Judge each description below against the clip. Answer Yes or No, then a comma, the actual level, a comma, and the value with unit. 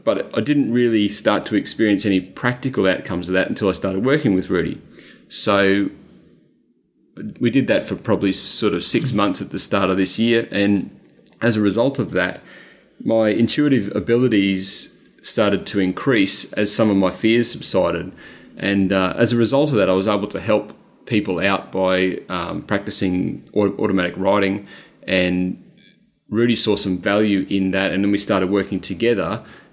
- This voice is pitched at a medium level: No, low, 100 Hz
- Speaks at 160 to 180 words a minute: Yes, average, 170 wpm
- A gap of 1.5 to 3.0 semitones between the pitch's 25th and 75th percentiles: Yes, average, 2.7 semitones